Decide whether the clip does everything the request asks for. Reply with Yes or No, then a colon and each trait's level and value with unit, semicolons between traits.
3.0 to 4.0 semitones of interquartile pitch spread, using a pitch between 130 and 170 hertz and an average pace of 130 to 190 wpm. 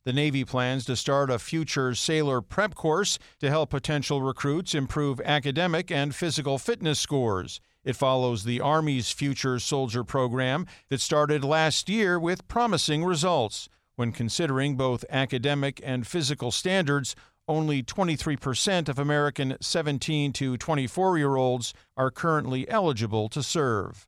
Yes: average, 3.4 semitones; medium, 140 Hz; slow, 135 wpm